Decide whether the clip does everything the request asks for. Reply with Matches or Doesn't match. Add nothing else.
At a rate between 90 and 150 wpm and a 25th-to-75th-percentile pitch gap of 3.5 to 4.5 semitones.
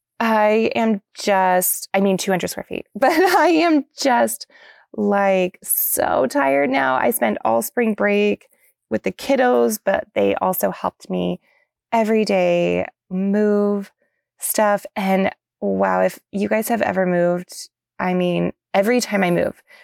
Matches